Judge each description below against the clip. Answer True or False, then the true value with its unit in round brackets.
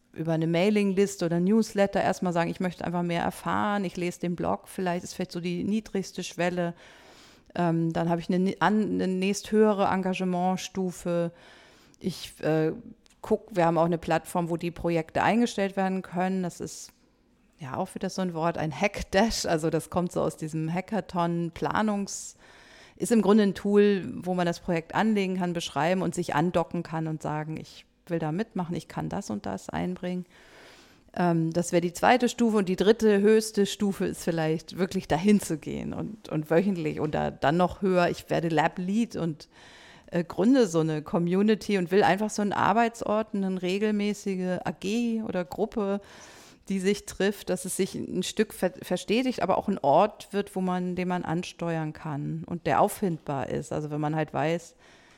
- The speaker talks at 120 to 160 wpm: False (185 wpm)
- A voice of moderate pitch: True (180 Hz)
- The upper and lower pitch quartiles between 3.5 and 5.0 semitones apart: False (3.0 semitones)